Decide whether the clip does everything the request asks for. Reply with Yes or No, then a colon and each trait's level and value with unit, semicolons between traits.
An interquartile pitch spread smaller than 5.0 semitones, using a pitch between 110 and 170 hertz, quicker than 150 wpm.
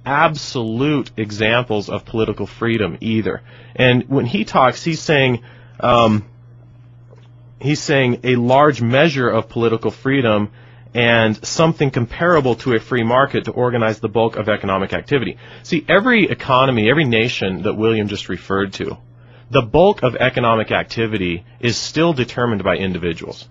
No: narrow, 2.5 semitones; low, 120 Hz; average, 140 wpm